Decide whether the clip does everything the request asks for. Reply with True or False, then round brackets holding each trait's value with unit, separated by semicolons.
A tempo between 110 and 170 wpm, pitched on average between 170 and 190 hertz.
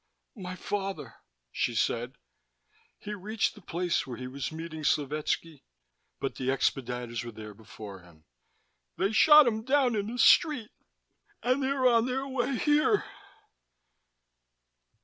True (135 wpm; 185 Hz)